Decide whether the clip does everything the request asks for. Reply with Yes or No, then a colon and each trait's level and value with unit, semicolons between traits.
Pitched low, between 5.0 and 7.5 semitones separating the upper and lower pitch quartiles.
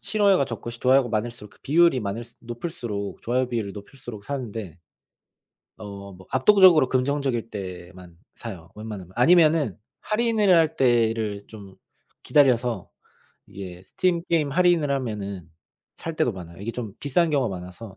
Yes: low, 120 Hz; wide, 6.2 semitones